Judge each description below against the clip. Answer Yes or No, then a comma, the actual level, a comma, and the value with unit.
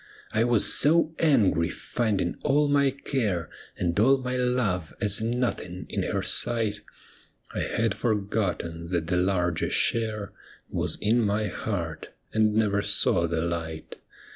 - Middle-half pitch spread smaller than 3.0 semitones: No, average, 5.1 semitones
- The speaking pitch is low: Yes, low, 105 Hz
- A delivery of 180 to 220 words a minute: No, average, 140 wpm